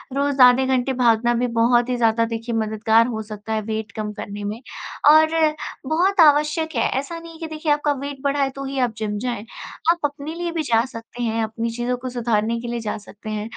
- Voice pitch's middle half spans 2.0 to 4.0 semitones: No, average, 4.4 semitones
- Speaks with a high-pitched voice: Yes, high, 240 Hz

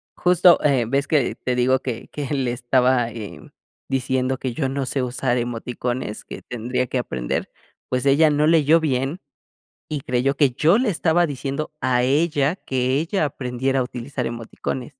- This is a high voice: No, low, 130 Hz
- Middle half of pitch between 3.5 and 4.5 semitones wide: No, average, 3.0 semitones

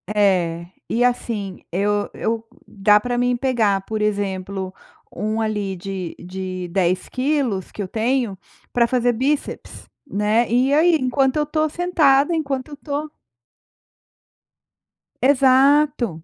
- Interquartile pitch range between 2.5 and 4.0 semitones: No, wide, 5.6 semitones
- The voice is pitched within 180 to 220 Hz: No, high, 230 Hz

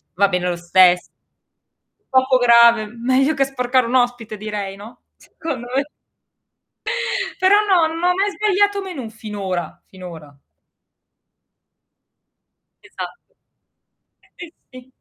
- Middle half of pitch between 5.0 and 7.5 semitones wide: Yes, wide, 5.6 semitones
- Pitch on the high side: Yes, high, 240 Hz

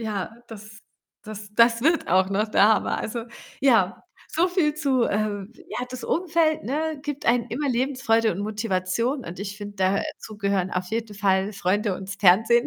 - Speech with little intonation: No, average, 4.3 semitones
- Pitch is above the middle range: Yes, high, 220 Hz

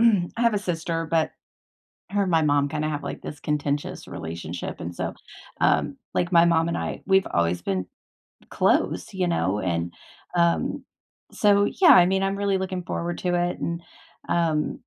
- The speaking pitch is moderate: Yes, medium, 170 Hz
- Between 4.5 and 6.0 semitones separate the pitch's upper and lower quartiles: Yes, average, 4.8 semitones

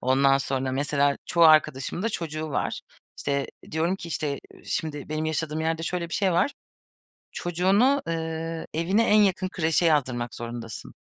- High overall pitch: No, medium, 160 Hz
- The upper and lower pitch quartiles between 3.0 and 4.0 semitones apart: Yes, average, 3.6 semitones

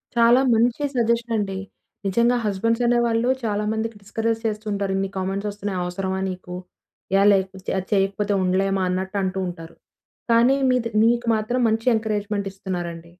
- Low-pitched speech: No, high, 205 Hz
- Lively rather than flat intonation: No, average, 3.2 semitones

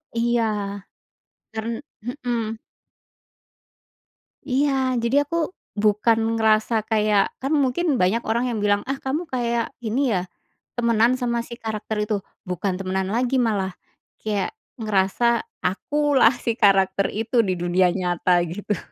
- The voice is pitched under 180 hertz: No, high, 225 Hz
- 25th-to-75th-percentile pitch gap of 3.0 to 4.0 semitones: Yes, average, 3.4 semitones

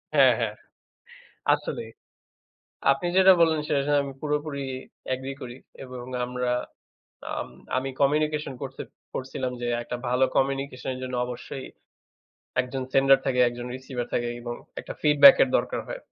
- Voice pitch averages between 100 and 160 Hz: Yes, low, 135 Hz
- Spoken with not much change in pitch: Yes, narrow, 2.2 semitones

